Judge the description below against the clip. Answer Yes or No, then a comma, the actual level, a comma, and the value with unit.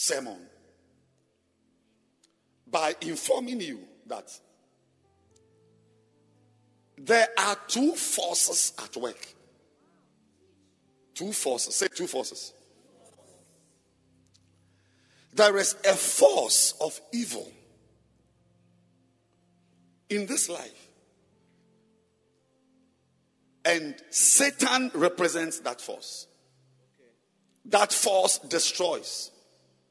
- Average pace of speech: No, slow, 65 wpm